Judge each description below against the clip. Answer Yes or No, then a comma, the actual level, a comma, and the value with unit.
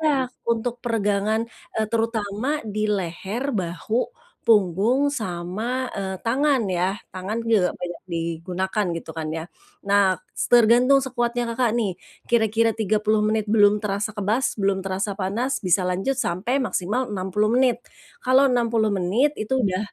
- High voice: Yes, high, 215 Hz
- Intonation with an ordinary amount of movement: Yes, average, 3.8 semitones